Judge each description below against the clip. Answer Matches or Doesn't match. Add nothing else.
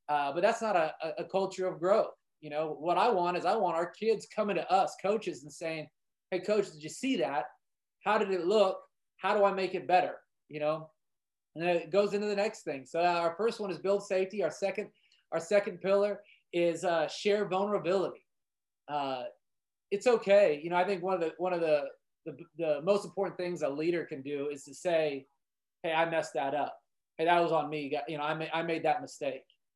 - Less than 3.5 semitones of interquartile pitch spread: Doesn't match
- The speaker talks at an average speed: Doesn't match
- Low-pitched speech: Doesn't match